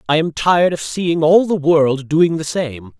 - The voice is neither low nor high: Yes, medium, 160 Hz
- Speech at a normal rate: No, fast, 220 wpm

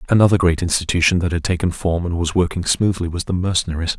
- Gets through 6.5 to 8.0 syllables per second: Yes, 6.6 syllables/s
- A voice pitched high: No, very low, 85 Hz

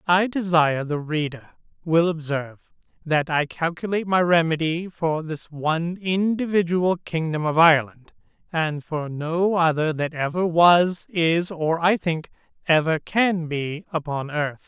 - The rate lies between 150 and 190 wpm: No, average, 140 wpm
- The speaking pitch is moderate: Yes, medium, 165 Hz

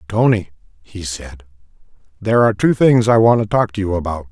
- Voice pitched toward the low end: Yes, low, 100 Hz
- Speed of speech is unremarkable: Yes, average, 195 wpm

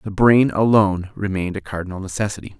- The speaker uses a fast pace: No, average, 160 wpm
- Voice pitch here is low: Yes, low, 100 Hz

